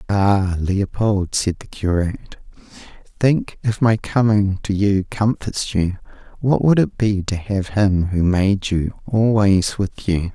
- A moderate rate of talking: Yes, average, 150 wpm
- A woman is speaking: No, male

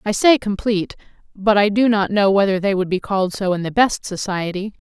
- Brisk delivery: Yes, fast, 220 wpm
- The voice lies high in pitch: Yes, high, 200 Hz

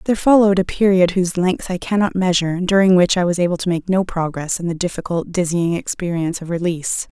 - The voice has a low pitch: No, medium, 180 Hz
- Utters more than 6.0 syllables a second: Yes, 6.5 syllables/s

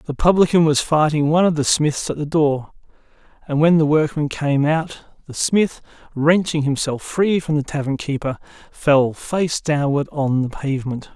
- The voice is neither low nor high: Yes, medium, 150 Hz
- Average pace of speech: Yes, average, 170 wpm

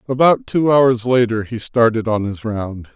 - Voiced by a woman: No, male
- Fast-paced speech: No, average, 185 wpm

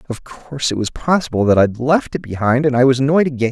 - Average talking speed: No, fast, 255 wpm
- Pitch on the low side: Yes, low, 130 Hz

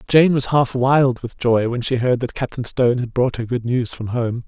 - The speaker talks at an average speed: No, fast, 255 wpm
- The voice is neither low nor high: No, low, 125 Hz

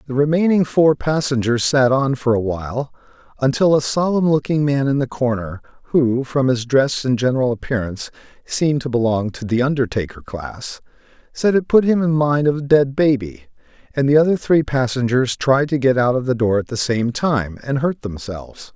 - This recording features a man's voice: Yes, male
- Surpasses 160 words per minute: Yes, average, 190 wpm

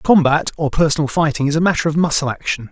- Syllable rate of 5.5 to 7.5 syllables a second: Yes, 6.5 syllables/s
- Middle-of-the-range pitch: Yes, medium, 155 Hz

